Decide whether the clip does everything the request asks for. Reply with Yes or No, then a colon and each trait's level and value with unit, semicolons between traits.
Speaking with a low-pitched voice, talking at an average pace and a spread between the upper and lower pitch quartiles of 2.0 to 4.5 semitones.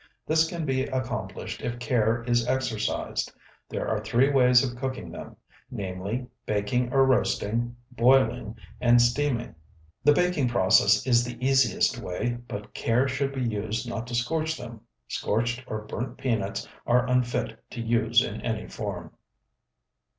Yes: low, 120 Hz; average, 145 wpm; average, 2.7 semitones